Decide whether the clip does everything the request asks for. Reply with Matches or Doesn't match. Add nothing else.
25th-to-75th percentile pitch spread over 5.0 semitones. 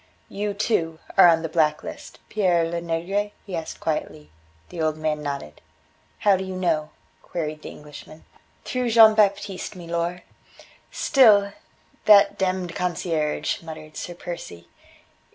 Doesn't match